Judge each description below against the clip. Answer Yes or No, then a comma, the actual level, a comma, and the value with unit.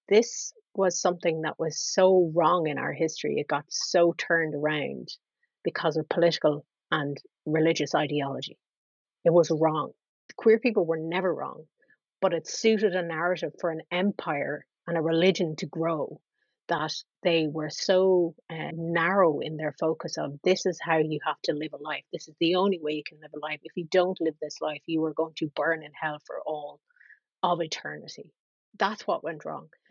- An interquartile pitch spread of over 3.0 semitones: No, narrow, 2.6 semitones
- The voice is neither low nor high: Yes, medium, 165 Hz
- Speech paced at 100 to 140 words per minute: No, average, 185 wpm